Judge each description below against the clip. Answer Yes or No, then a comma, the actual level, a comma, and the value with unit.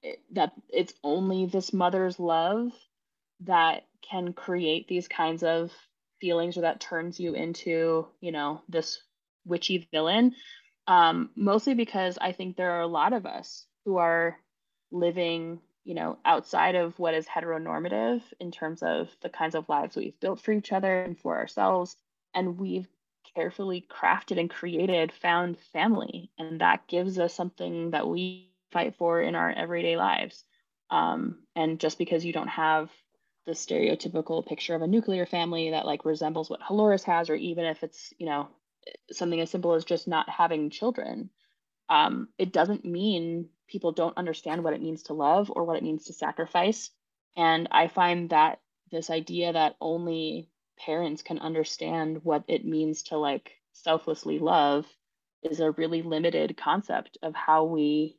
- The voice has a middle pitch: Yes, medium, 170 Hz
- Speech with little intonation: Yes, narrow, 2.2 semitones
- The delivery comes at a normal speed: Yes, average, 165 wpm